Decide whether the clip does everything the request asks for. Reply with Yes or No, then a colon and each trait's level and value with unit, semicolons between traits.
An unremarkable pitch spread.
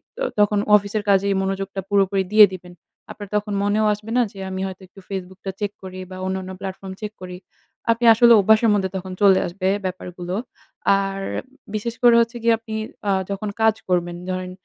No: narrow, 2.1 semitones